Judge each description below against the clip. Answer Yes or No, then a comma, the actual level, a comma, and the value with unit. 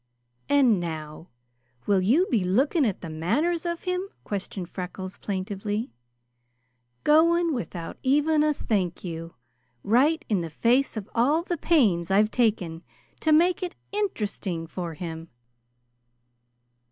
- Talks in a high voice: Yes, high, 215 Hz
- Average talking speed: No, slow, 130 wpm